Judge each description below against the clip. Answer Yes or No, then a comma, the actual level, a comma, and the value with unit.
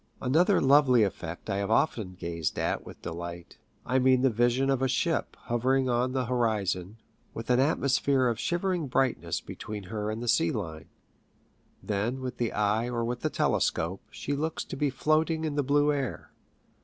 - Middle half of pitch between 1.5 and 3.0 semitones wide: No, average, 4.5 semitones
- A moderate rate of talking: Yes, average, 180 wpm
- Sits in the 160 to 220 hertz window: No, low, 125 Hz